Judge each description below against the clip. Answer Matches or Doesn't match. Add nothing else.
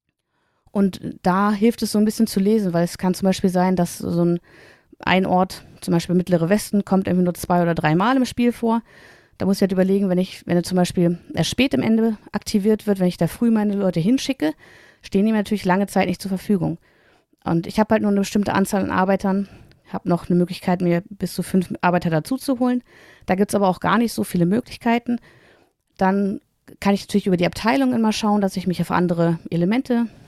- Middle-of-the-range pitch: Doesn't match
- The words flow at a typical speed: Doesn't match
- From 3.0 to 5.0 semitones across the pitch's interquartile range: Matches